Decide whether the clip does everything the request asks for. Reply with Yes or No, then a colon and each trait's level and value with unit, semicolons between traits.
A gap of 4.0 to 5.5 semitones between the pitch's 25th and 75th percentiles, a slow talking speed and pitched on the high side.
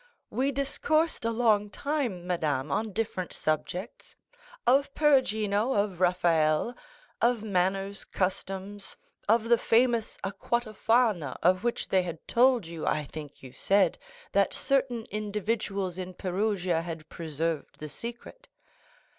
Yes: average, 5.0 semitones; slow, 125 wpm; high, 200 Hz